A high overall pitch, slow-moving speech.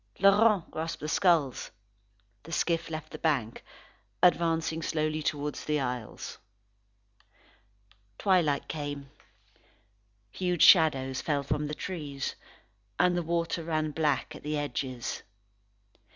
No: medium, 155 Hz; slow, 110 wpm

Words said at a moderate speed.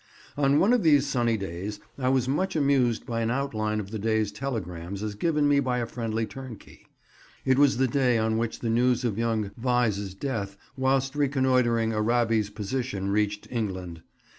Yes: average, 175 wpm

